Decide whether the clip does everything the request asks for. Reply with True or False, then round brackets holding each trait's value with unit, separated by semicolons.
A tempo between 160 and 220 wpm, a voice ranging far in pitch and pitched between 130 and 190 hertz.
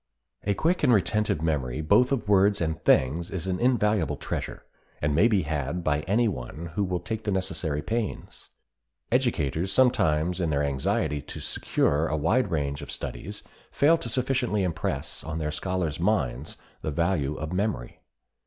False (165 wpm; 5.8 semitones; 90 Hz)